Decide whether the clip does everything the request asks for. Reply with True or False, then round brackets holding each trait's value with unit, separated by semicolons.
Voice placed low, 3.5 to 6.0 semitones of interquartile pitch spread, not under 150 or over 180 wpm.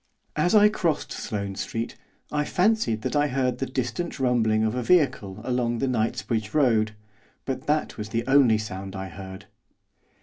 True (120 Hz; 4.7 semitones; 165 wpm)